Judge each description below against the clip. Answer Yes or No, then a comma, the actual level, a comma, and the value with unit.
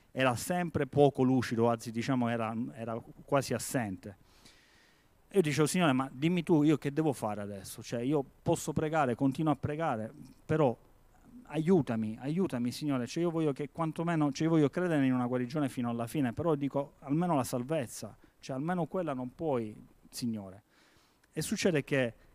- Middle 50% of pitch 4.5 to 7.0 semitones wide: Yes, average, 4.8 semitones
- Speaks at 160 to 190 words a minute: Yes, average, 165 wpm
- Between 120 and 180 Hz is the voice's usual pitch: Yes, medium, 140 Hz